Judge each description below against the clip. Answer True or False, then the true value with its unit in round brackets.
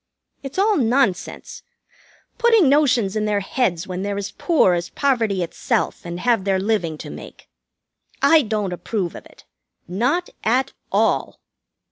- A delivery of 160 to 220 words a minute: False (145 wpm)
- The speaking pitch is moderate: False (215 Hz)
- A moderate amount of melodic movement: False (6.3 semitones)